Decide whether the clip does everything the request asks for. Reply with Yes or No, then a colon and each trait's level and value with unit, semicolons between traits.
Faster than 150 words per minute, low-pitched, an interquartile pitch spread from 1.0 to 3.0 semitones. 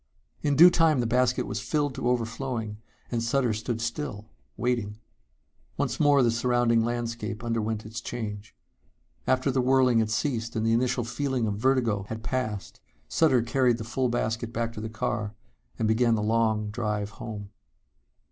Yes: average, 165 wpm; low, 115 Hz; narrow, 2.4 semitones